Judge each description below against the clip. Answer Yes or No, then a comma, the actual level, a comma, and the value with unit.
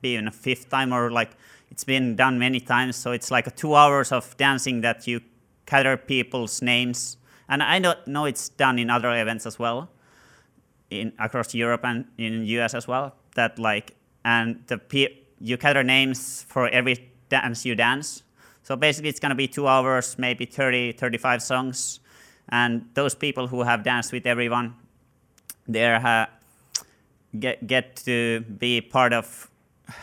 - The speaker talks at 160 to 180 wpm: Yes, average, 170 wpm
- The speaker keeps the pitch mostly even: Yes, narrow, 2.0 semitones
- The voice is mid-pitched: No, low, 125 Hz